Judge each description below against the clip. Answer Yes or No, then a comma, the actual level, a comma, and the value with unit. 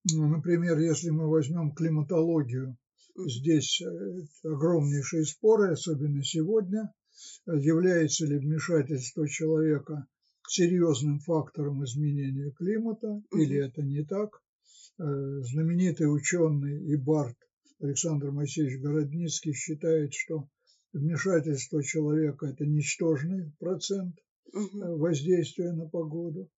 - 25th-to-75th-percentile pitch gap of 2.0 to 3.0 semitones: Yes, narrow, 2.5 semitones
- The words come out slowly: Yes, slow, 90 wpm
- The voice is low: No, medium, 155 Hz